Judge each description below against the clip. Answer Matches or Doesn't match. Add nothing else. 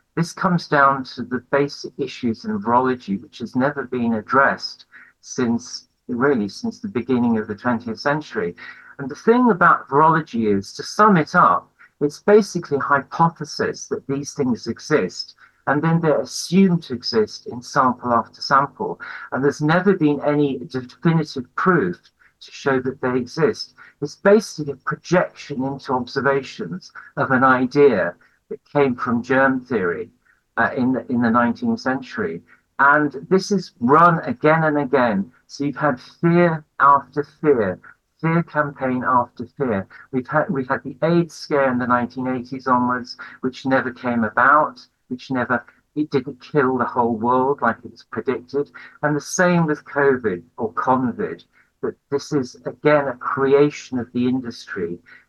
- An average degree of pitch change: Matches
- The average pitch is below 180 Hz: Matches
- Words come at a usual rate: Matches